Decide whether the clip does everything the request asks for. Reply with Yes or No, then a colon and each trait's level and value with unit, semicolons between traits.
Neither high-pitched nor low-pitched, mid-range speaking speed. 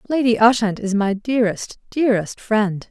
No: high, 220 Hz; average, 145 wpm